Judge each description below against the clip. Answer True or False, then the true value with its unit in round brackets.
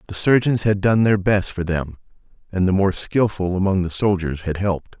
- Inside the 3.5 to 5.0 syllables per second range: False (5.2 syllables/s)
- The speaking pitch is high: False (95 Hz)